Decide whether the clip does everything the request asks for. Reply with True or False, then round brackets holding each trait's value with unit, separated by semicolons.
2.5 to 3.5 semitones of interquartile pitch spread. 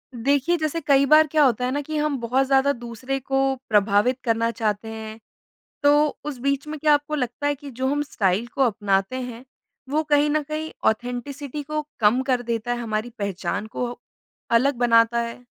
False (3.9 semitones)